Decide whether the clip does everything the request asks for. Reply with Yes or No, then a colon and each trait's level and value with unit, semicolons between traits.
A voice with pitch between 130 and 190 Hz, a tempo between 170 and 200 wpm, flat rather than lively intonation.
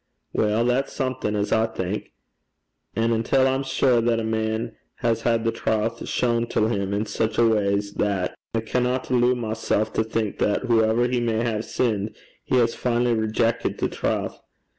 No: low, 115 Hz; average, 180 wpm; narrow, 1.7 semitones